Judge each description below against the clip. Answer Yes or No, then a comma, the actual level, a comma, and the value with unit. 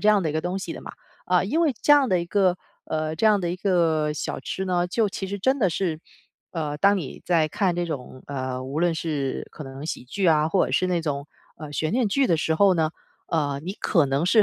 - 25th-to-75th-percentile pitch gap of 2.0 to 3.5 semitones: No, average, 4.1 semitones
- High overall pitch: No, medium, 170 Hz